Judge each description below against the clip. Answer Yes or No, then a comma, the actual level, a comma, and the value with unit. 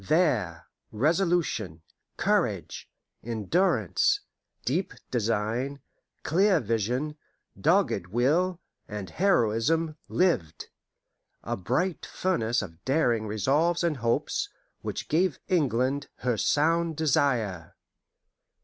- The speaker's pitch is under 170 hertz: Yes, low, 135 Hz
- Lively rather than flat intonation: Yes, wide, 7.3 semitones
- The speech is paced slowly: Yes, slow, 85 wpm